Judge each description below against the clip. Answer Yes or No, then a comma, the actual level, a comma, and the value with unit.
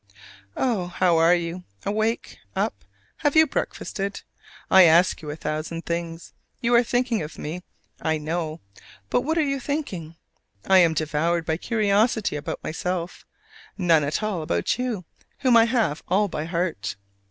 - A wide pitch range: Yes, wide, 5.7 semitones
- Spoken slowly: No, average, 155 wpm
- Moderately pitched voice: Yes, medium, 180 Hz